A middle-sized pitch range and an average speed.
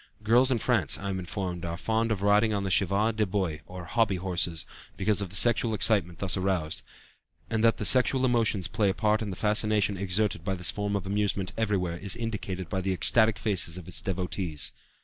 No: average, 3.0 semitones; fast, 210 wpm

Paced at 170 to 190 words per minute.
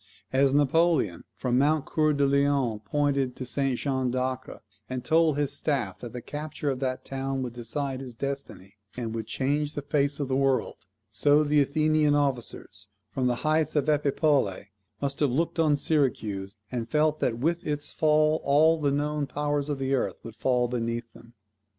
Yes: average, 180 wpm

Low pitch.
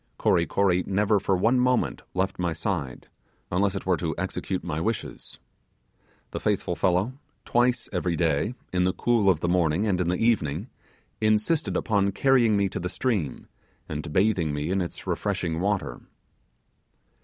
Yes: very low, 95 Hz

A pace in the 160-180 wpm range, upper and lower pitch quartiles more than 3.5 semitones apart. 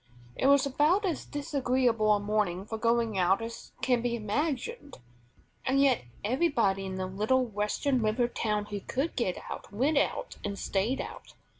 Yes: average, 165 wpm; average, 4.8 semitones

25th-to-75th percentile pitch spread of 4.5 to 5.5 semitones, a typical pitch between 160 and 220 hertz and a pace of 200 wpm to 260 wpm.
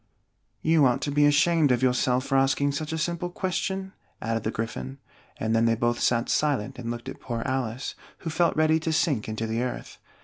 No: average, 5.2 semitones; low, 135 Hz; fast, 205 wpm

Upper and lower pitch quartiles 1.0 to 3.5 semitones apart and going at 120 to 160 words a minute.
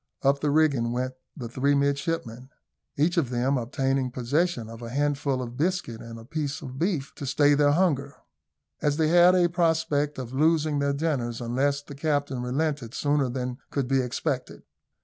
No: average, 3.2 semitones; average, 175 wpm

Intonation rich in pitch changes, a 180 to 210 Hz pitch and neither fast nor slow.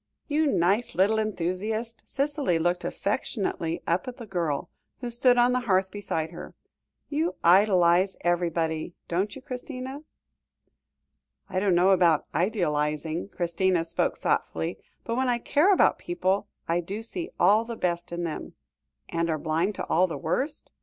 Yes: wide, 5.8 semitones; high, 190 Hz; average, 155 wpm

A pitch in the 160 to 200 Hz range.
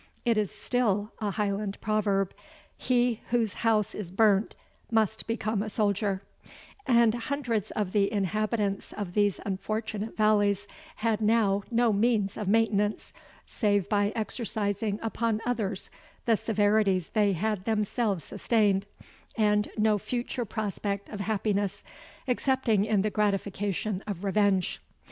No: high, 210 Hz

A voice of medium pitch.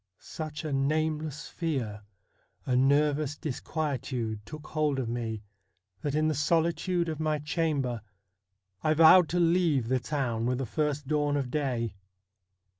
Yes: medium, 150 Hz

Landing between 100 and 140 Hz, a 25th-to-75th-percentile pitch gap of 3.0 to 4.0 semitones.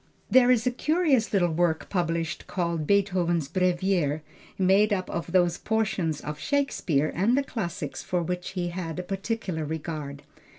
No: medium, 180 Hz; average, 3.7 semitones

